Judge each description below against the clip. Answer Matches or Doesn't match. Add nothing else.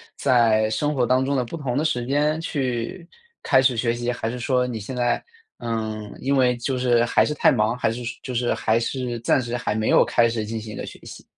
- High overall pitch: Doesn't match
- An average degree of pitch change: Doesn't match